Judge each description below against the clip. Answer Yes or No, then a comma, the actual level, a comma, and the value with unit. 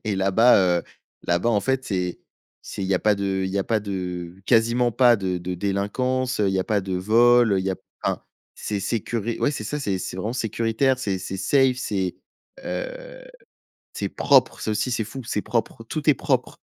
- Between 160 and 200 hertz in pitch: No, low, 105 Hz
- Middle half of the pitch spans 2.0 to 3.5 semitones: No, average, 4.2 semitones